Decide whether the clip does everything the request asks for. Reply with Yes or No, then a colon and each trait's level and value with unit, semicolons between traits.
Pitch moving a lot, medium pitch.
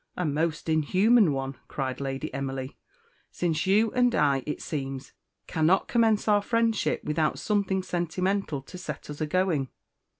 Yes: wide, 6.1 semitones; medium, 165 Hz